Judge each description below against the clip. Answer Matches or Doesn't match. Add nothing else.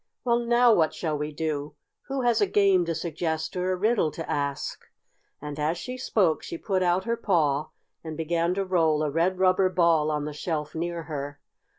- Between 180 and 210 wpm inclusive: Matches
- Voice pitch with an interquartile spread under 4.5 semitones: Matches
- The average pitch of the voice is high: Doesn't match